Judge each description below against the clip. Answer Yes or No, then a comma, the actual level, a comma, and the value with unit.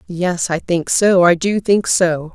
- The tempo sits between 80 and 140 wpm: No, fast, 205 wpm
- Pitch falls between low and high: Yes, medium, 180 Hz